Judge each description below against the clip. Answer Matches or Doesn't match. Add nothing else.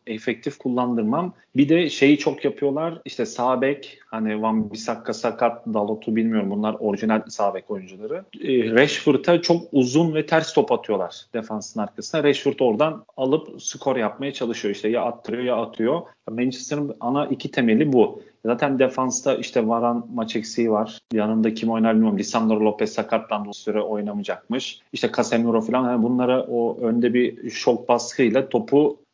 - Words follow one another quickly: Matches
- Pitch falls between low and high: Doesn't match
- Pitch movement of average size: Matches